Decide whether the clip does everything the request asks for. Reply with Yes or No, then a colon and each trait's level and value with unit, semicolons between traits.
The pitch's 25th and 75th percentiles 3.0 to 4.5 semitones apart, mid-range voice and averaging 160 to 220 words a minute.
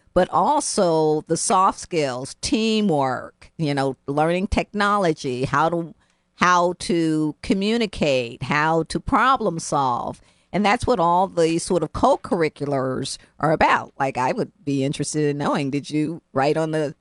No: average, 4.1 semitones; medium, 160 Hz; average, 150 wpm